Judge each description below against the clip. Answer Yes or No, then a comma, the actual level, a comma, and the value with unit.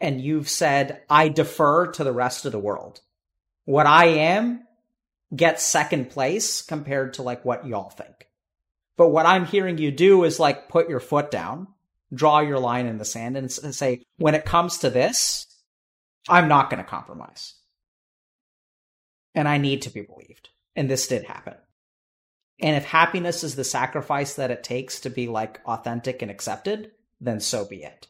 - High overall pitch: No, medium, 140 Hz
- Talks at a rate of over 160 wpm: Yes, average, 175 wpm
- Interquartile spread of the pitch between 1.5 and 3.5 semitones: No, average, 5.1 semitones